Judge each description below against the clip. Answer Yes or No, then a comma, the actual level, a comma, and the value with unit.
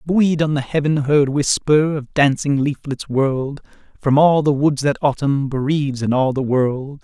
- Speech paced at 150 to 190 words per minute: Yes, average, 180 wpm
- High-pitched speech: No, medium, 140 Hz